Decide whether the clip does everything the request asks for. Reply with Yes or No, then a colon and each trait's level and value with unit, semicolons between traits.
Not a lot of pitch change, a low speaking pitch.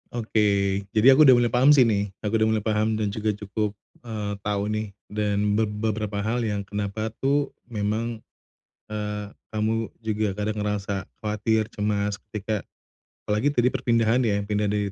Yes: narrow, 1.4 semitones; low, 105 Hz